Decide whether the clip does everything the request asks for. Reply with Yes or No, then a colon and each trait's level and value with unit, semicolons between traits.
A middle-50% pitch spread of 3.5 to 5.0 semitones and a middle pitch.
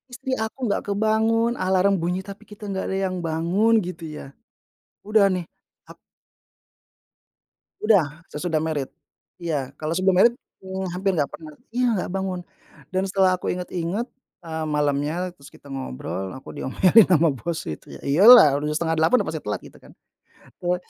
Yes: average, 4.1 semitones; medium, 180 Hz